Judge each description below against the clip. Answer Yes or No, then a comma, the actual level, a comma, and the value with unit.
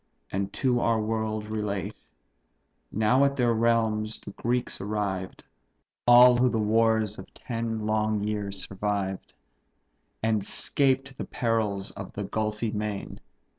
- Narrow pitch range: Yes, narrow, 2.0 semitones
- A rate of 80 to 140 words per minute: Yes, slow, 135 wpm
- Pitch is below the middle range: Yes, low, 110 Hz